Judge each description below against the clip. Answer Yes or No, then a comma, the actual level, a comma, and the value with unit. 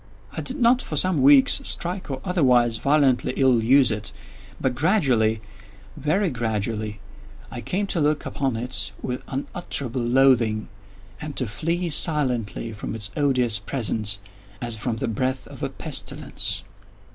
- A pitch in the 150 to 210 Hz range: No, low, 125 Hz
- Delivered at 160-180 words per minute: No, slow, 135 wpm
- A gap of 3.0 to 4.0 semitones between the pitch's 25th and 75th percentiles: No, average, 4.9 semitones